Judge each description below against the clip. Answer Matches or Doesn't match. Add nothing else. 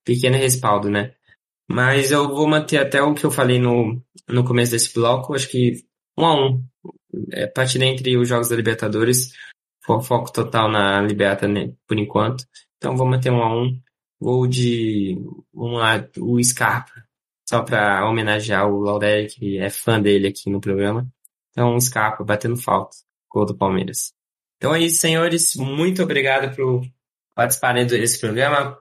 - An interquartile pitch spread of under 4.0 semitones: Matches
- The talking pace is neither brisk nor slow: Matches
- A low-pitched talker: Matches